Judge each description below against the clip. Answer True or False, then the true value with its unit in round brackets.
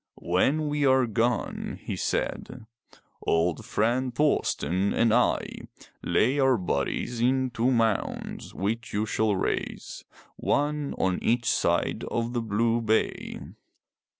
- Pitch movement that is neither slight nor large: True (3.4 semitones)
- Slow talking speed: True (125 wpm)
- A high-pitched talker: False (115 Hz)